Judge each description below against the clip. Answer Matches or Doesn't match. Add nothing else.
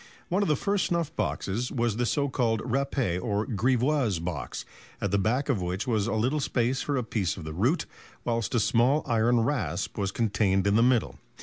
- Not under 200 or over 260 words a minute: Matches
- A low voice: Matches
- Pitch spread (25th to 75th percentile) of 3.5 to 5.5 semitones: Matches